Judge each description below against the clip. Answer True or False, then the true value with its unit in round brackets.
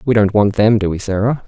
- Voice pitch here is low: True (105 Hz)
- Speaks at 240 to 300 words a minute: True (285 wpm)